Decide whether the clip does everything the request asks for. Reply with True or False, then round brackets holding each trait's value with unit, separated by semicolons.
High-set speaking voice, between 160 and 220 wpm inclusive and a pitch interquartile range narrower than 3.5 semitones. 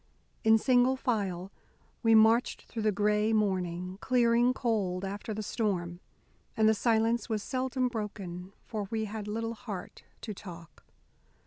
False (215 Hz; 140 wpm; 2.9 semitones)